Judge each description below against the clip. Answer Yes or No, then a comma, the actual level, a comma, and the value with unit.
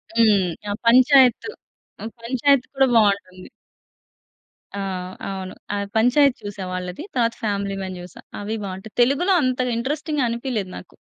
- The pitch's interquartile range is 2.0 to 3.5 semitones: No, average, 4.7 semitones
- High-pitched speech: Yes, high, 230 Hz